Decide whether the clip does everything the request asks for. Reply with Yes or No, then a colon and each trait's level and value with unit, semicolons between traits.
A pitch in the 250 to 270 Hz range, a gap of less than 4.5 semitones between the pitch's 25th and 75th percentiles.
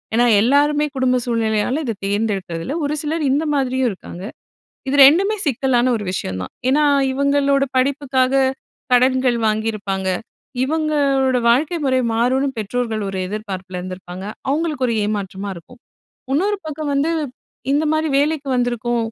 No: very high, 255 Hz; average, 4.8 semitones